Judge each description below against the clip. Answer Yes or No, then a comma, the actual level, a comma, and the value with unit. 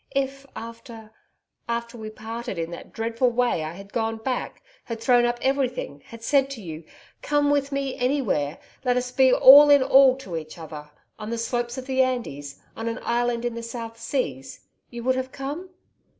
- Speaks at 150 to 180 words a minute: No, average, 190 wpm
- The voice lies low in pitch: No, high, 240 Hz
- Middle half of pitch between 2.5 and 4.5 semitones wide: Yes, average, 2.9 semitones